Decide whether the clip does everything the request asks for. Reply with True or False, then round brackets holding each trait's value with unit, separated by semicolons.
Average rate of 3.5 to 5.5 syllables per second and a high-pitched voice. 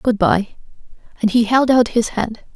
True (4.4 syllables/s; 230 Hz)